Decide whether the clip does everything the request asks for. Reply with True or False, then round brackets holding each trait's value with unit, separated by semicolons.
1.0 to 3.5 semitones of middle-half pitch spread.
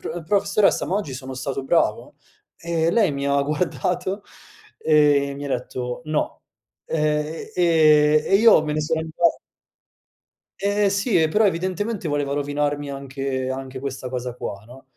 False (4.1 semitones)